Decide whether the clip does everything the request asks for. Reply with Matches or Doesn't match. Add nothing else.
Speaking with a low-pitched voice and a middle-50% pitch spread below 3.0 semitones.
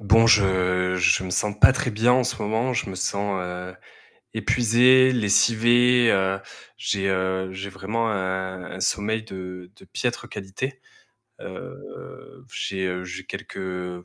Doesn't match